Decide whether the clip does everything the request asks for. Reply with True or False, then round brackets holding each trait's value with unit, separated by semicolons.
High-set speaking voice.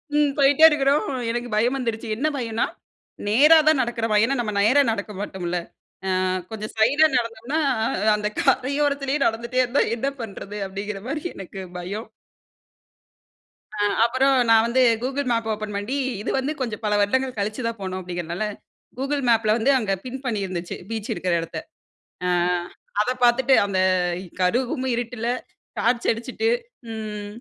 True (230 Hz)